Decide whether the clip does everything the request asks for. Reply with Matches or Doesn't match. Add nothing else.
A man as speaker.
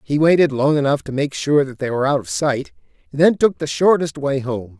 Matches